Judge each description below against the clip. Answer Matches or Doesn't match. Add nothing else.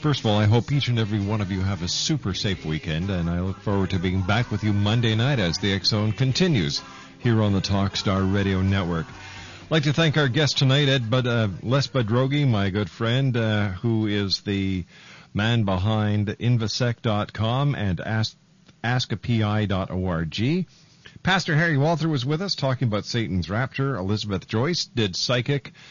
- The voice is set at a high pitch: Doesn't match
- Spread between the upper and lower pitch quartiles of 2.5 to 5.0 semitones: Doesn't match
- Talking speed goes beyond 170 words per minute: Matches